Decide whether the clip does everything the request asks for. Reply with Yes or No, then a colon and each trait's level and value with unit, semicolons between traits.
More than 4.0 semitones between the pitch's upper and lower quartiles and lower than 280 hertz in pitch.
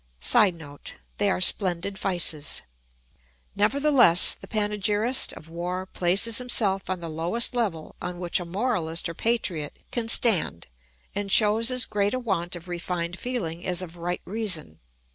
Yes: average, 4.5 semitones; medium, 185 Hz